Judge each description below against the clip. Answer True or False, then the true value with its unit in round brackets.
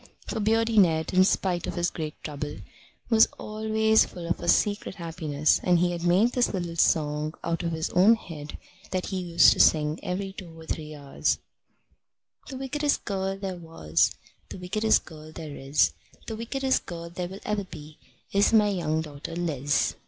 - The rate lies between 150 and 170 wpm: False (180 wpm)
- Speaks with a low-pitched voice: False (175 Hz)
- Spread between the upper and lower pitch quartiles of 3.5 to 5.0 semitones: True (4.5 semitones)